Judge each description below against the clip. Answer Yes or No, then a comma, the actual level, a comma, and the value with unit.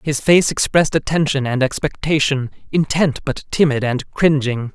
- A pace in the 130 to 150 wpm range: Yes, average, 140 wpm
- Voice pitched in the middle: Yes, medium, 145 Hz